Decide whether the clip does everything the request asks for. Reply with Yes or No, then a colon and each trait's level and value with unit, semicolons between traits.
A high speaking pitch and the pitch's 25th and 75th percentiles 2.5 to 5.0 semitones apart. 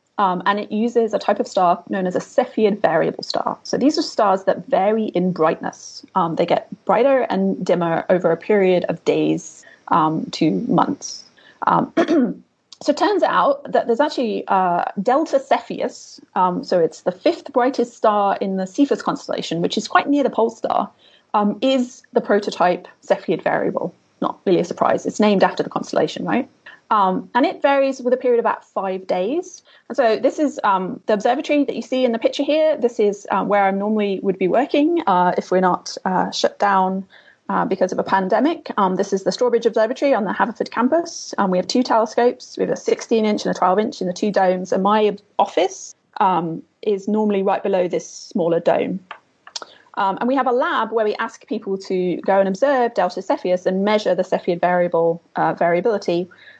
No: high, 215 Hz; wide, 5.4 semitones